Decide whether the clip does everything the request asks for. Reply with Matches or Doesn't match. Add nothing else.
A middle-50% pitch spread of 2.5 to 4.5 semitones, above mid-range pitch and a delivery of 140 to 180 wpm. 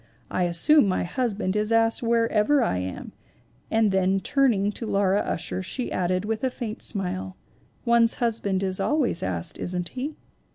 Matches